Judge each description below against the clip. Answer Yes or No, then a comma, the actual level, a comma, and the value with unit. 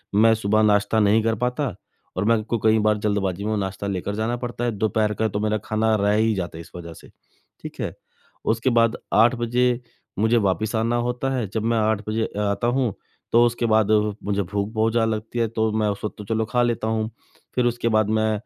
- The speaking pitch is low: Yes, low, 110 Hz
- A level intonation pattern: Yes, narrow, 2.0 semitones